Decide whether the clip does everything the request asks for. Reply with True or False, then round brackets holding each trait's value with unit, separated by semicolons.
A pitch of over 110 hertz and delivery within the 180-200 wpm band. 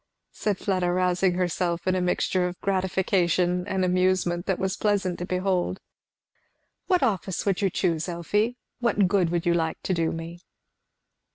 False (185 Hz; 160 wpm)